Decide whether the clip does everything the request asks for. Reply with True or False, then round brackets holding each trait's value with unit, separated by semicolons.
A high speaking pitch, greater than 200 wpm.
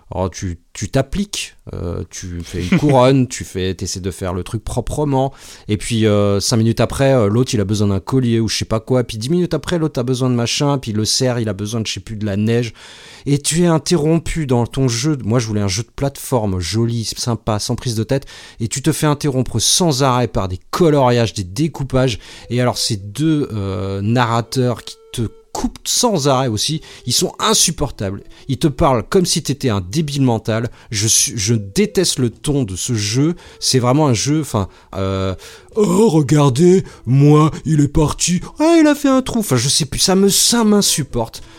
False (125 Hz; 215 wpm)